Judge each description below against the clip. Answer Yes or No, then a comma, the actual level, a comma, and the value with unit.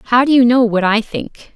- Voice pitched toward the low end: No, high, 235 Hz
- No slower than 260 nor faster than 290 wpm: Yes, fast, 270 wpm